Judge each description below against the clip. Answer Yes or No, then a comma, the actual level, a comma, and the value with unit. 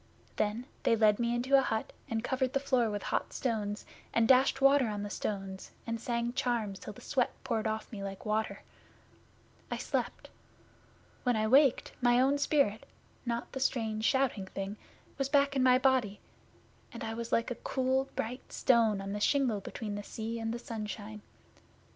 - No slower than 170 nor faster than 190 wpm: Yes, average, 180 wpm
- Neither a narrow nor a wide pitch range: Yes, average, 3.4 semitones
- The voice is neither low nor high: No, high, 230 Hz